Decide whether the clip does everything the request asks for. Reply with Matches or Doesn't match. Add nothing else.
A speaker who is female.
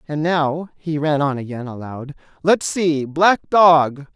Doesn't match